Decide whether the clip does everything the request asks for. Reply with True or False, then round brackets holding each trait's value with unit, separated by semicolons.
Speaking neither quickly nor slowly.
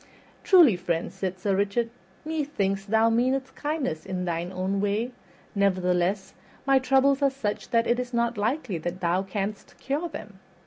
True (160 wpm)